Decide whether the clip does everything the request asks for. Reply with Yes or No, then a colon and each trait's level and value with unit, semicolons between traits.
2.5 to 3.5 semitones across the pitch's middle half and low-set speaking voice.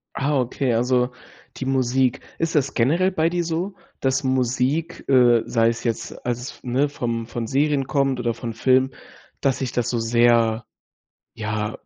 Yes: average, 2.8 semitones; low, 130 Hz